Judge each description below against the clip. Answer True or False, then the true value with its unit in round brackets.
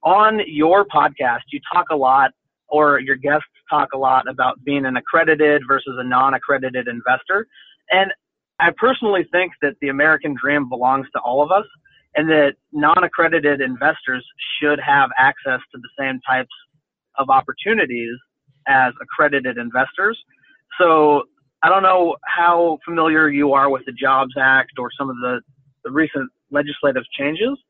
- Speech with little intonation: False (3.8 semitones)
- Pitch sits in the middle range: True (145 Hz)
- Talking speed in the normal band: True (150 wpm)